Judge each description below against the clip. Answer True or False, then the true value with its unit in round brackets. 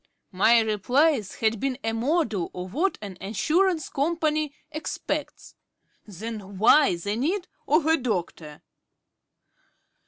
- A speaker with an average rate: False (120 wpm)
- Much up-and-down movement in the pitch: True (7.3 semitones)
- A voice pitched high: True (230 Hz)